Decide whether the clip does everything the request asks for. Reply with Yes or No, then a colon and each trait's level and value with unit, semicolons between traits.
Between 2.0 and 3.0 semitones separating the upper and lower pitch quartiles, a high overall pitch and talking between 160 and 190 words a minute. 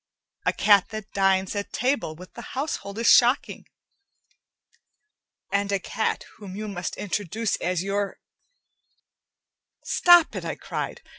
No: average, 2.7 semitones; high, 200 Hz; slow, 135 wpm